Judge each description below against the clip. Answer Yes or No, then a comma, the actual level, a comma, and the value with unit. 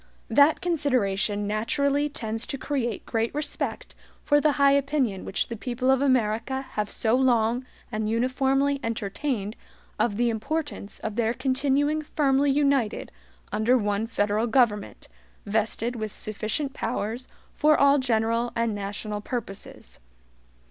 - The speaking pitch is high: Yes, high, 240 Hz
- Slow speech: Yes, slow, 130 wpm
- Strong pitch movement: No, average, 4.3 semitones